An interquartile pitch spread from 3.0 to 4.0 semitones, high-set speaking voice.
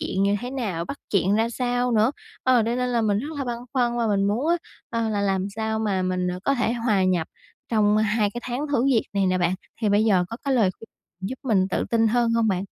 Yes: average, 3.5 semitones; high, 220 Hz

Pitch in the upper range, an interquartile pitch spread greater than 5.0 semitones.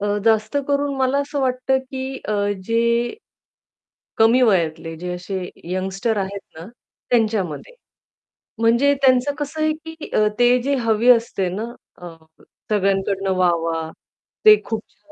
Yes: high, 225 Hz; wide, 5.4 semitones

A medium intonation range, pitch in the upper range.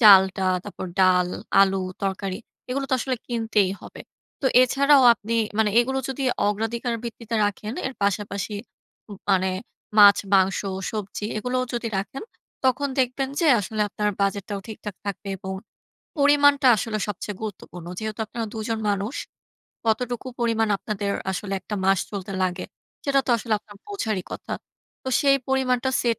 Yes: average, 4.0 semitones; high, 215 Hz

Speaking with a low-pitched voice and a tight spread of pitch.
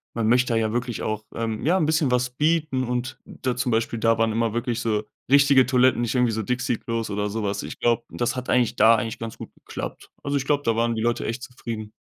Yes: low, 120 Hz; narrow, 2.1 semitones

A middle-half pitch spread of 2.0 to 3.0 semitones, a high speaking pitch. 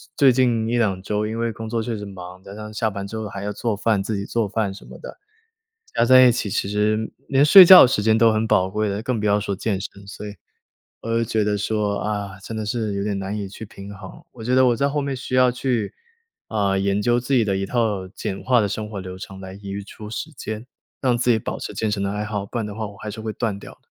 No: narrow, 2.5 semitones; low, 105 Hz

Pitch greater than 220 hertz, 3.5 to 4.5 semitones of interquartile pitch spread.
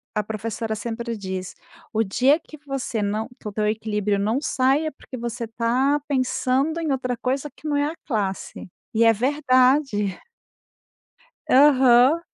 Yes: high, 245 Hz; average, 4.1 semitones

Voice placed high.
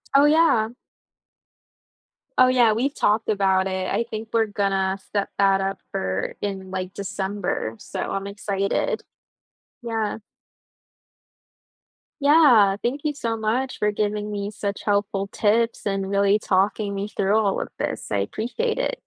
Yes: high, 205 Hz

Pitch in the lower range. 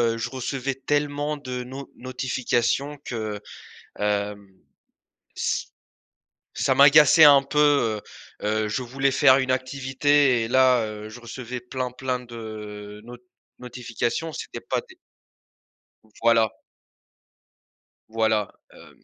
Yes: low, 125 Hz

